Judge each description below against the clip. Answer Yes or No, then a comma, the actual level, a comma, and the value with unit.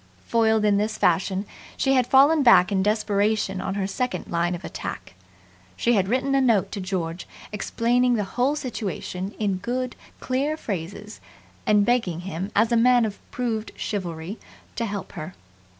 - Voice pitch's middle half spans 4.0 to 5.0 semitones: Yes, average, 4.3 semitones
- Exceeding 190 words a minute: No, average, 165 wpm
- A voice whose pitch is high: Yes, high, 210 Hz